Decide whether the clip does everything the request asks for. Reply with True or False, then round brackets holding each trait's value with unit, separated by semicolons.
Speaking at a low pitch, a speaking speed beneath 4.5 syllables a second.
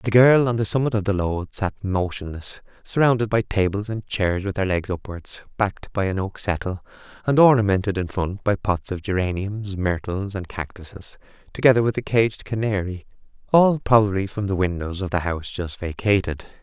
False (100 Hz; 5.2 syllables/s)